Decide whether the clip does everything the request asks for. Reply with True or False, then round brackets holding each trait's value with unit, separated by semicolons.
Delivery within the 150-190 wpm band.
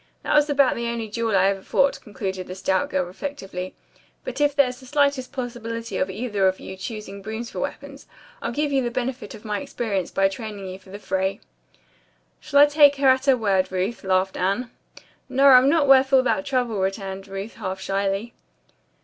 False (200 wpm)